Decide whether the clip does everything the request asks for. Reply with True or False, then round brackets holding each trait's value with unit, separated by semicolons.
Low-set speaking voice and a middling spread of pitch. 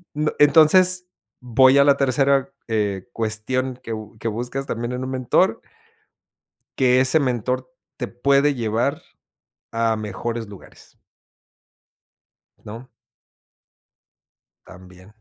True (125 Hz; 3.5 semitones)